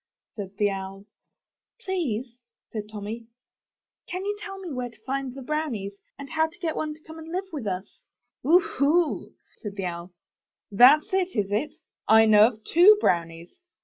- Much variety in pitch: Yes, wide, 7.5 semitones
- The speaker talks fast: No, average, 175 wpm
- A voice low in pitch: No, very high, 250 Hz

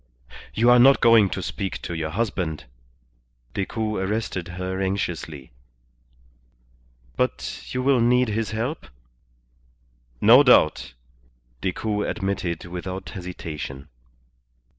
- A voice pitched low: Yes, very low, 95 Hz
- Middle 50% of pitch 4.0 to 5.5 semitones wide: Yes, average, 4.5 semitones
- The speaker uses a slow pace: Yes, slow, 100 wpm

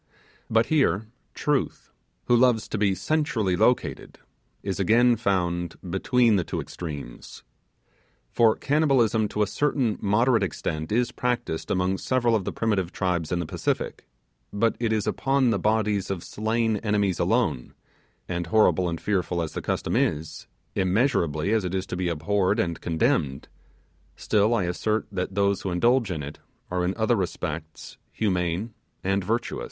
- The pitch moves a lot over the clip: No, average, 4.4 semitones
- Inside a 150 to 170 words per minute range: Yes, average, 155 wpm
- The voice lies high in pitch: No, low, 100 Hz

